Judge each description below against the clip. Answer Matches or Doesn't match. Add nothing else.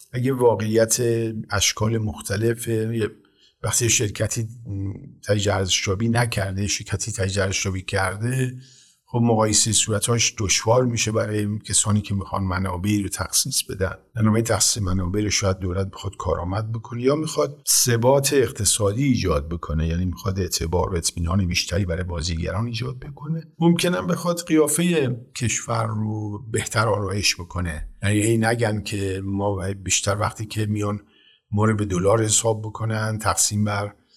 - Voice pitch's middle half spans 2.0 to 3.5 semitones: Matches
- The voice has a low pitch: Matches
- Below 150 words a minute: Matches